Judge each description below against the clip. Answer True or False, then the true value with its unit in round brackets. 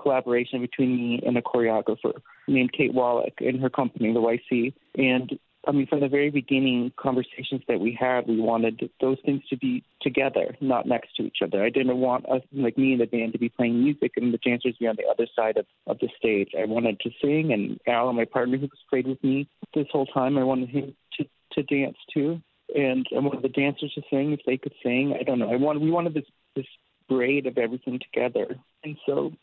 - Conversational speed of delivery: False (230 wpm)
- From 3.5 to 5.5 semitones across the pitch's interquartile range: False (2.5 semitones)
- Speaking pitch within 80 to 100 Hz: False (130 Hz)